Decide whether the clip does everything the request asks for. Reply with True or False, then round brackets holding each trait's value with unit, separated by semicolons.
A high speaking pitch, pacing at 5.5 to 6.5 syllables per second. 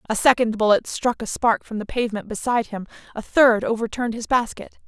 True (230 Hz; 6.0 syllables/s)